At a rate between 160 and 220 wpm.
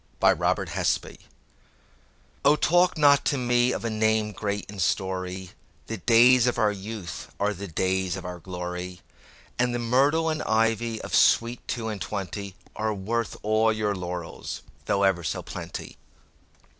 No: average, 145 wpm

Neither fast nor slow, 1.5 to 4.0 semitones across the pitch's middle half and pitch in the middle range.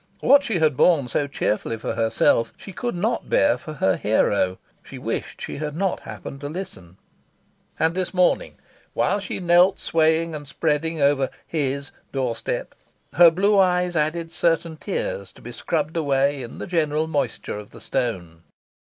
No: average, 165 wpm; average, 4.6 semitones; medium, 155 Hz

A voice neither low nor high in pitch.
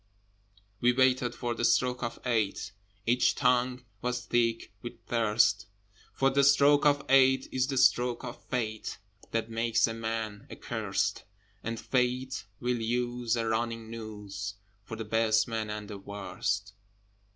No: low, 115 Hz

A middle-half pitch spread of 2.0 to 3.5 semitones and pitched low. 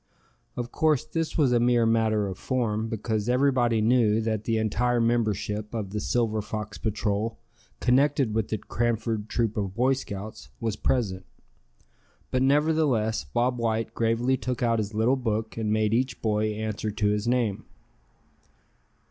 Yes: narrow, 2.4 semitones; low, 115 Hz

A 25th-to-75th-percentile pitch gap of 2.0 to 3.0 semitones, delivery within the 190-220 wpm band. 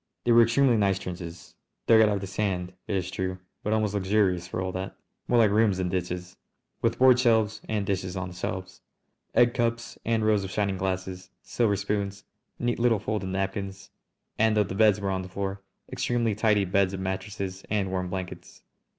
Yes: narrow, 2.5 semitones; average, 195 wpm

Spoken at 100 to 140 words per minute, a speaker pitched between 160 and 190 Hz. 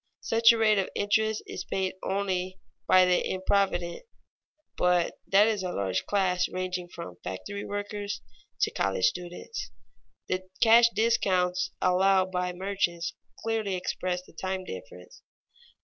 Yes: slow, 135 wpm; medium, 185 Hz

